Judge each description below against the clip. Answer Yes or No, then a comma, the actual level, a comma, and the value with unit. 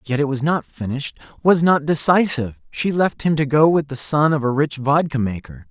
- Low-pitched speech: No, medium, 150 Hz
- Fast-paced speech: Yes, fast, 220 wpm